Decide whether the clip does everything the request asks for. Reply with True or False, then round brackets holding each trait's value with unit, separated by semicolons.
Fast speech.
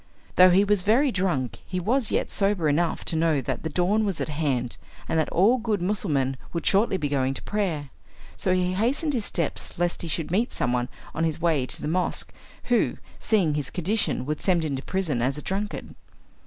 True (210 wpm)